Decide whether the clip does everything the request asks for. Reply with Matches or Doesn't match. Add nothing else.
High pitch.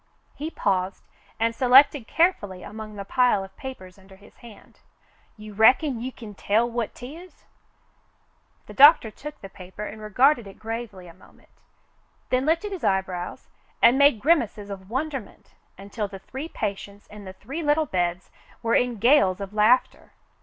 Matches